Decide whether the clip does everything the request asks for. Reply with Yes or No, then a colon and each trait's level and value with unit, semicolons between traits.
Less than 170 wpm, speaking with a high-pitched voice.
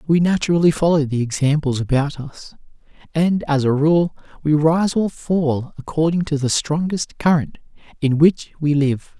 No: average, 155 wpm; medium, 155 Hz